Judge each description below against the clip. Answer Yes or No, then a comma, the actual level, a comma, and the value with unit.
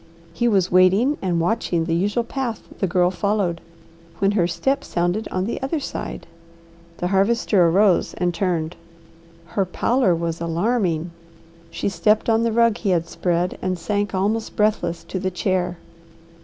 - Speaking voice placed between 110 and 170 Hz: No, high, 190 Hz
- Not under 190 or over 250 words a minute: No, average, 155 wpm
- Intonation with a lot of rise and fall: No, average, 3.8 semitones